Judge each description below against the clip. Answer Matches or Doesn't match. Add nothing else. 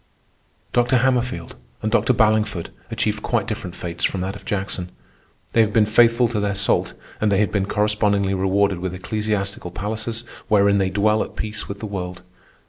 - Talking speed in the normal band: Matches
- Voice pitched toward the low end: Matches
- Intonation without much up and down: Matches